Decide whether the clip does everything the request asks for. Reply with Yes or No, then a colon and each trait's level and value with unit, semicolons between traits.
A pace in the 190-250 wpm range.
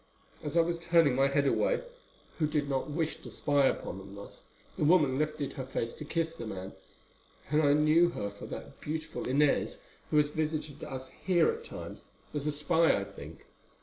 Yes: average, 195 wpm